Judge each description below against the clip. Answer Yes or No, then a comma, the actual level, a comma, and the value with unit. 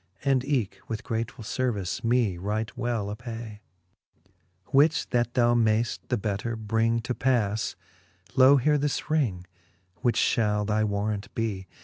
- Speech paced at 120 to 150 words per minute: Yes, average, 140 wpm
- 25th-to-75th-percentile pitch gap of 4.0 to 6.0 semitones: No, average, 3.0 semitones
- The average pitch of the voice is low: Yes, low, 115 Hz